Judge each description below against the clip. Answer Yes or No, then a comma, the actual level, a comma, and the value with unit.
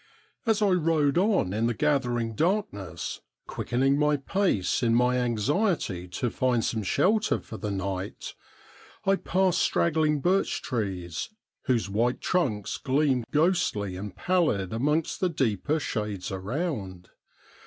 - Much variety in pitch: Yes, wide, 8.0 semitones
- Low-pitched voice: Yes, low, 125 Hz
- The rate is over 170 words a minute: No, slow, 135 wpm